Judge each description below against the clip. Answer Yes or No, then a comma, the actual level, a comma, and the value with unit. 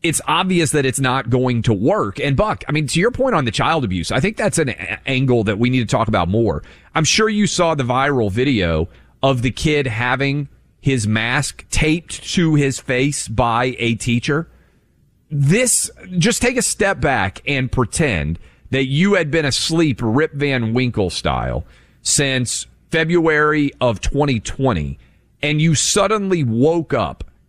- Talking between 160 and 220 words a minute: Yes, average, 170 wpm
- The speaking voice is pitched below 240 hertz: Yes, low, 135 Hz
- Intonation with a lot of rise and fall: Yes, wide, 5.7 semitones